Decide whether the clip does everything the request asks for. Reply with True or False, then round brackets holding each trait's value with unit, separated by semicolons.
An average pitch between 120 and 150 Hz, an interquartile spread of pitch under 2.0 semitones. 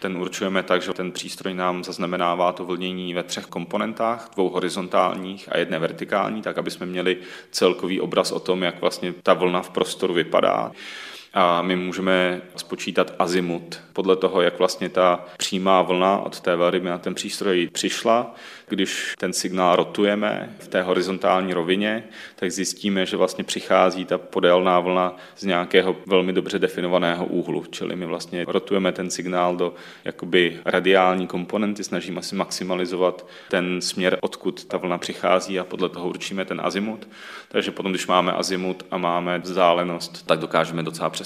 False (90 Hz; 0.9 semitones)